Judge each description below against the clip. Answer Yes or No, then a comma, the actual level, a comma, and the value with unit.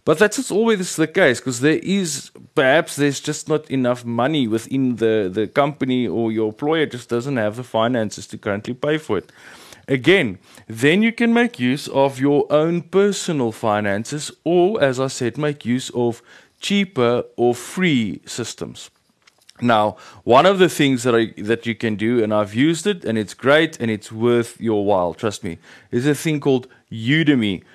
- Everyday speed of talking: Yes, average, 180 wpm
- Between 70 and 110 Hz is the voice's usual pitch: No, low, 130 Hz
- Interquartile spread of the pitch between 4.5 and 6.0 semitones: Yes, average, 5.2 semitones